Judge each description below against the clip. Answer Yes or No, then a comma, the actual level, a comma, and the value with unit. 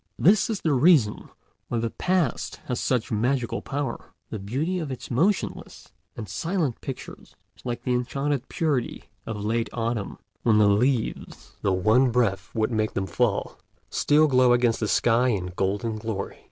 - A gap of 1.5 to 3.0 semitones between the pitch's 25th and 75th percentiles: No, average, 4.2 semitones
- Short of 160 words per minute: No, average, 165 wpm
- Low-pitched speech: Yes, low, 120 Hz